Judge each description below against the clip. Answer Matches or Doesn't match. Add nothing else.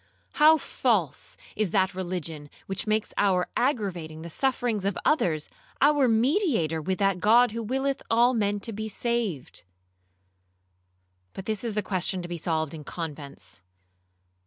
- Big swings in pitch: Matches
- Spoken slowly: Doesn't match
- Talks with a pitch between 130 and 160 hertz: Doesn't match